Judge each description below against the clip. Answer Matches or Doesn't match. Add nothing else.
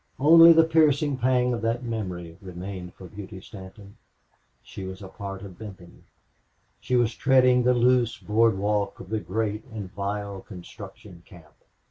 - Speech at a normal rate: Matches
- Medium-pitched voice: Doesn't match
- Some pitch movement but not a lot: Matches